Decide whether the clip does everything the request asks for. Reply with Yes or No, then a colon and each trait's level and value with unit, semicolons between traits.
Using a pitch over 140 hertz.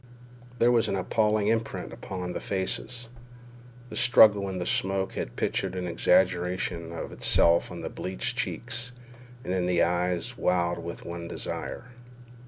No: very low, 95 Hz